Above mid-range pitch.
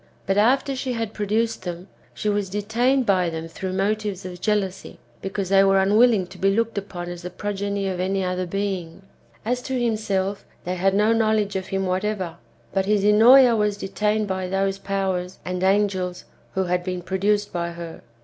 Yes: high, 195 Hz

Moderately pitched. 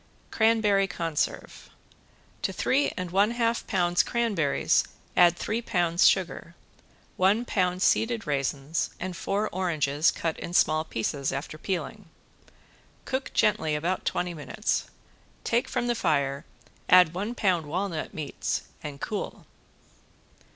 Yes: medium, 180 Hz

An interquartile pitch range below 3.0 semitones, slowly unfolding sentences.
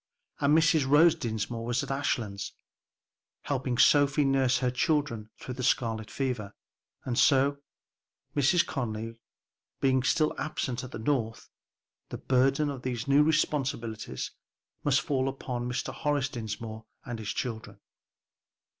No: average, 3.6 semitones; slow, 130 wpm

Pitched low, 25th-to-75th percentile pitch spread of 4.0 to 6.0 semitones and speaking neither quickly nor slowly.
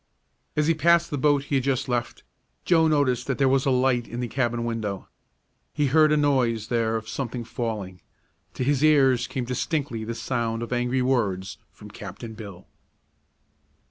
No: low, 125 Hz; average, 3.3 semitones; average, 180 wpm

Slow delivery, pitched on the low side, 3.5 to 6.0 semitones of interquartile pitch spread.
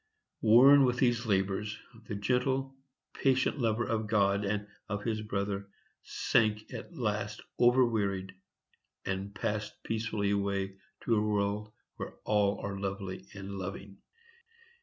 No: slow, 125 wpm; low, 105 Hz; narrow, 2.5 semitones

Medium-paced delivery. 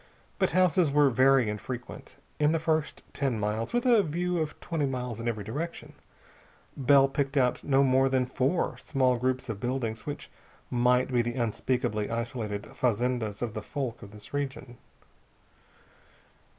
Yes: average, 155 wpm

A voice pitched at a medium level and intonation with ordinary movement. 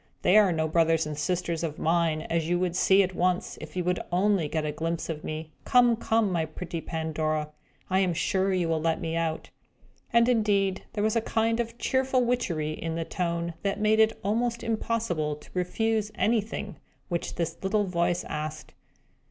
Yes: medium, 180 Hz; average, 4.7 semitones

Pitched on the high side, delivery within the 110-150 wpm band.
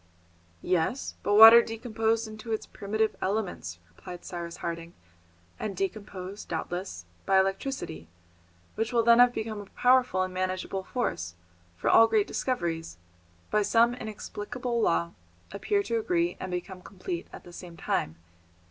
Yes: high, 200 Hz; average, 140 wpm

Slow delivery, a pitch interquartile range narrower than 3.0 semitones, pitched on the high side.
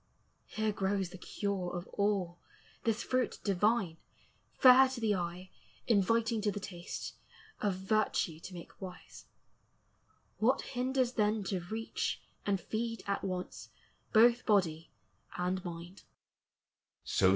No: slow, 120 wpm; average, 3.8 semitones; high, 200 Hz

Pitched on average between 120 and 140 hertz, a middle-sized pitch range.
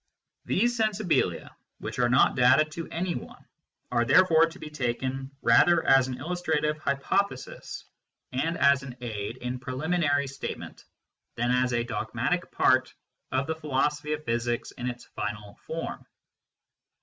Yes: low, 135 Hz; average, 4.5 semitones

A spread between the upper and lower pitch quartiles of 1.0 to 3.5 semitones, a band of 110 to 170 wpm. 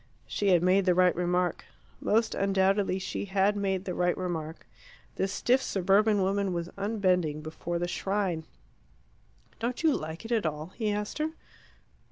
Yes: narrow, 2.6 semitones; average, 160 wpm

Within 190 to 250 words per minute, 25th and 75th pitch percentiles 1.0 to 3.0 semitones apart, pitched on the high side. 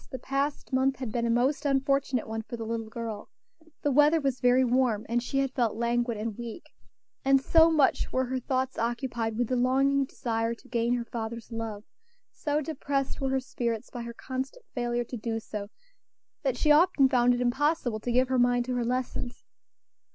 Yes: average, 195 wpm; narrow, 2.5 semitones; high, 245 Hz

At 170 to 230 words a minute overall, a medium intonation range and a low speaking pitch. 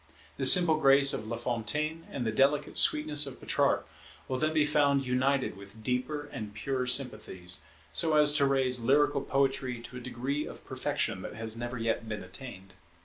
Yes: average, 175 wpm; average, 3.9 semitones; low, 130 Hz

